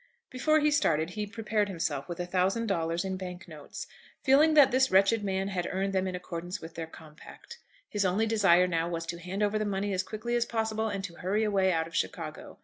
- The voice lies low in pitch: No, high, 190 Hz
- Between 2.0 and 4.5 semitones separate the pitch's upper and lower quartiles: Yes, average, 3.8 semitones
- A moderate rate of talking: No, fast, 225 wpm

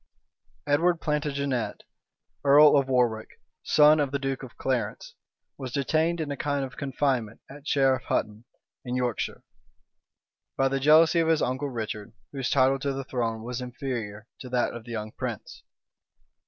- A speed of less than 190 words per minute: Yes, average, 155 wpm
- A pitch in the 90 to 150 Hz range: Yes, low, 135 Hz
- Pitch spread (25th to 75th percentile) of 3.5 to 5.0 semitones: No, average, 3.0 semitones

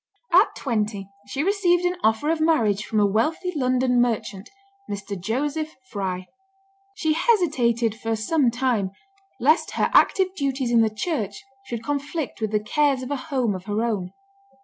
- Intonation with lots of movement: Yes, wide, 6.3 semitones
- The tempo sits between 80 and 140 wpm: No, average, 160 wpm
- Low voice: No, high, 245 Hz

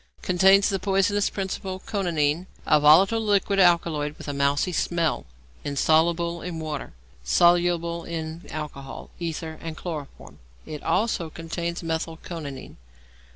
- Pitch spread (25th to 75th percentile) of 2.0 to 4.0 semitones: Yes, average, 2.7 semitones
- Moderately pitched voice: Yes, medium, 170 Hz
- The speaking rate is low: Yes, slow, 120 wpm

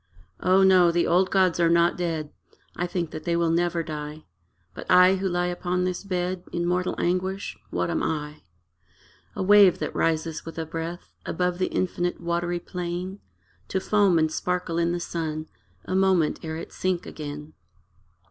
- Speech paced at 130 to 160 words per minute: No, average, 175 wpm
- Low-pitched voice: No, medium, 175 Hz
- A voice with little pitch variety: Yes, narrow, 1.8 semitones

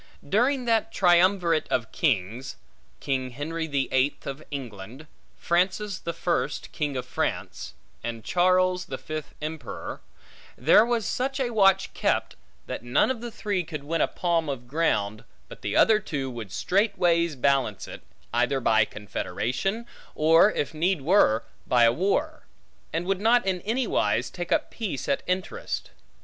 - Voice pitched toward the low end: No, medium, 165 Hz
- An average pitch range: No, wide, 6.9 semitones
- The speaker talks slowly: No, average, 155 wpm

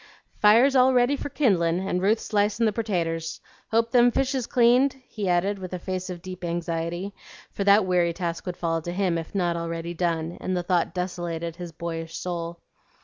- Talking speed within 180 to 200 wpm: Yes, average, 195 wpm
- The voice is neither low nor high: Yes, medium, 180 Hz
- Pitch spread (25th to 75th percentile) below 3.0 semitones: No, average, 3.8 semitones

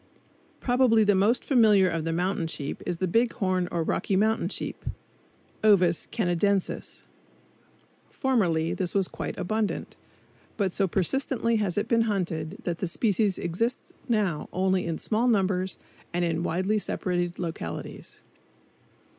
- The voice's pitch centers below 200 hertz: Yes, high, 190 Hz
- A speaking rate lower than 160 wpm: Yes, average, 140 wpm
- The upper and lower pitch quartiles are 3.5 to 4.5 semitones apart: Yes, average, 3.8 semitones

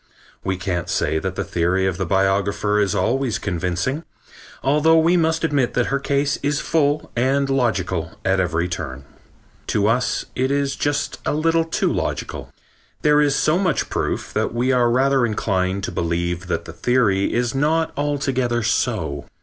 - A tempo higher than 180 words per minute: No, average, 165 wpm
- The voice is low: Yes, low, 120 Hz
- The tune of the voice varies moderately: No, wide, 7.1 semitones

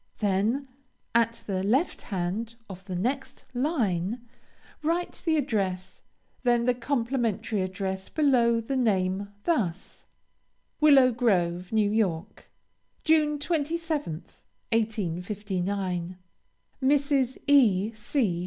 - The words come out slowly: Yes, slow, 95 wpm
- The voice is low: No, high, 225 Hz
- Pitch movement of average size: No, wide, 6.1 semitones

